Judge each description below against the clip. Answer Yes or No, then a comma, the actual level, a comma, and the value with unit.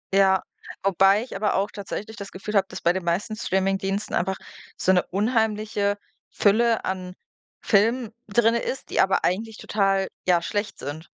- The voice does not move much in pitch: Yes, narrow, 2.1 semitones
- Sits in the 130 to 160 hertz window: No, high, 200 Hz